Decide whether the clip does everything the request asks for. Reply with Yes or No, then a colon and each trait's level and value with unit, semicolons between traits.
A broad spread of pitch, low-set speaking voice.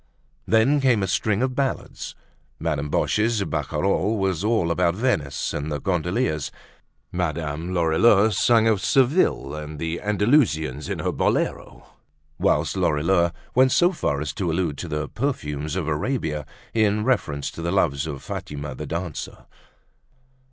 Yes: wide, 6.6 semitones; very low, 90 Hz